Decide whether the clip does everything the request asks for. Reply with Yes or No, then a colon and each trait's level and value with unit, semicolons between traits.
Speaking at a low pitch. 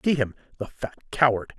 Yes: low, 120 Hz